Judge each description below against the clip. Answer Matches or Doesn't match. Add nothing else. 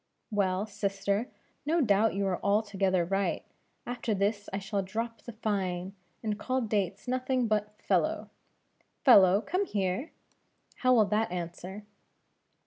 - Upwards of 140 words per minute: Doesn't match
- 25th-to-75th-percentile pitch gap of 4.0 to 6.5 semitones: Doesn't match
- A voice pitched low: Doesn't match